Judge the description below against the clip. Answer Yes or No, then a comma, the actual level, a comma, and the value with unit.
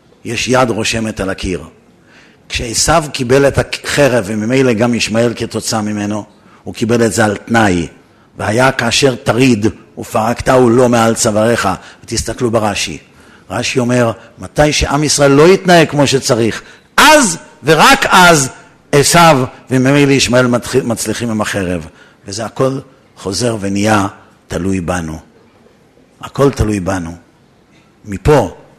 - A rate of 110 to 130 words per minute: Yes, average, 120 wpm